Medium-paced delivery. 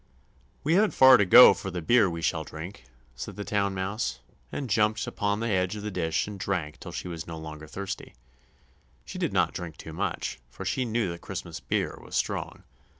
No: fast, 210 wpm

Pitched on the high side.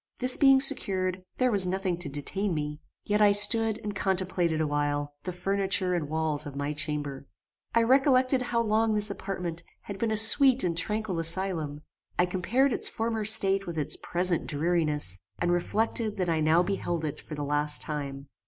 No: medium, 180 Hz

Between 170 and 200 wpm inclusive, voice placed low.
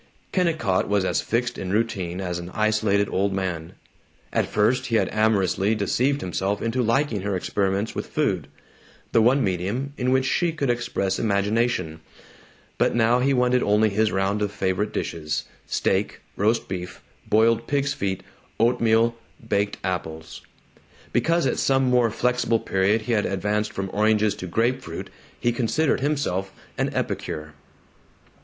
No: average, 150 wpm; low, 110 Hz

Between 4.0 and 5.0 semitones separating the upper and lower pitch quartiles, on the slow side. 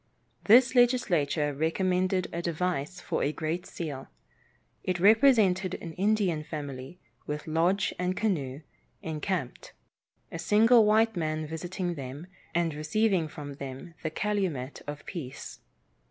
Yes: average, 4.4 semitones; slow, 125 wpm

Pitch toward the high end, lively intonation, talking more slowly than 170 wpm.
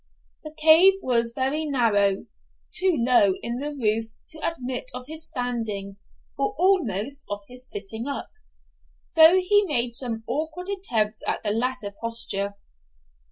Yes: very high, 250 Hz; wide, 6.0 semitones; average, 140 wpm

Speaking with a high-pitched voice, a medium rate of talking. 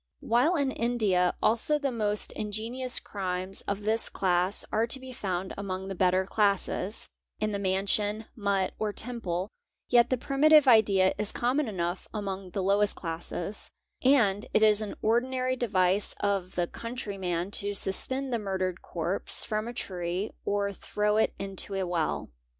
Yes: high, 205 Hz; average, 160 wpm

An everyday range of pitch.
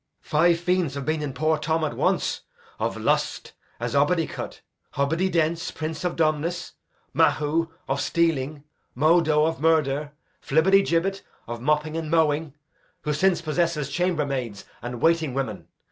No: narrow, 2.3 semitones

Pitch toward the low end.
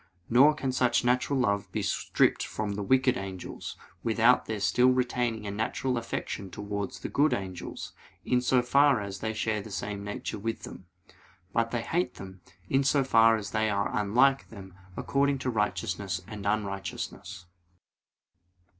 Yes: low, 110 Hz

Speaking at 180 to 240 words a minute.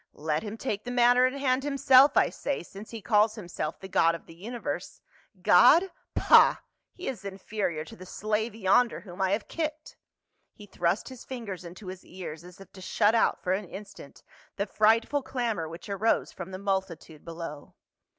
Yes: average, 190 wpm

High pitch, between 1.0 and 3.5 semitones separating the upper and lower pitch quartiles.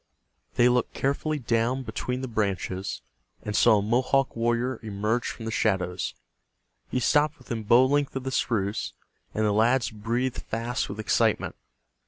No: low, 115 Hz; average, 3.2 semitones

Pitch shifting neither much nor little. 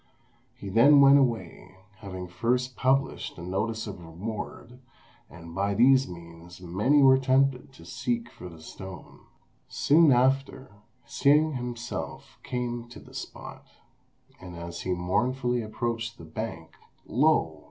No: wide, 6.2 semitones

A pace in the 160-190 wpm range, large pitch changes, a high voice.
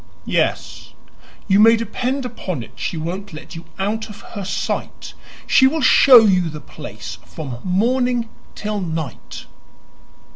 No: average, 140 wpm; wide, 6.4 semitones; high, 195 Hz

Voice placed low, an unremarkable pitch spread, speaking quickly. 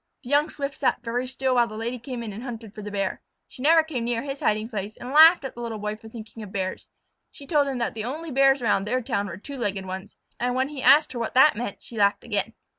No: high, 240 Hz; average, 4.1 semitones; fast, 270 wpm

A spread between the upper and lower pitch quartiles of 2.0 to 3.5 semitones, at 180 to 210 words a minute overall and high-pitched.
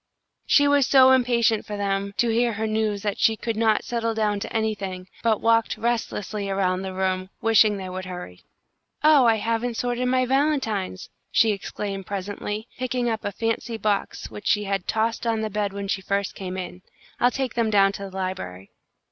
Yes: average, 2.8 semitones; average, 190 wpm; high, 215 Hz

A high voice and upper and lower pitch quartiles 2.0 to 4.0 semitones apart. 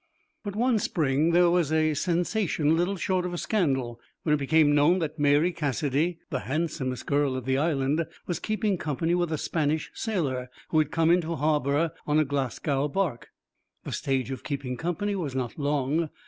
No: medium, 155 Hz; average, 3.7 semitones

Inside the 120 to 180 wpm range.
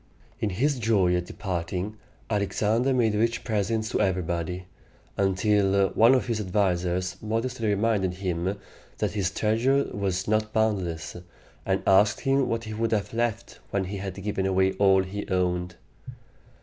Yes: average, 150 wpm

